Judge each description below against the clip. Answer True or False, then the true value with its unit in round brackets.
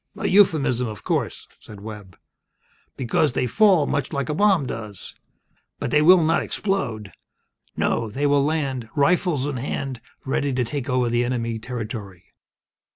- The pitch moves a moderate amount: True (4.6 semitones)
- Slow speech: False (155 wpm)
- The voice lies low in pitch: True (130 Hz)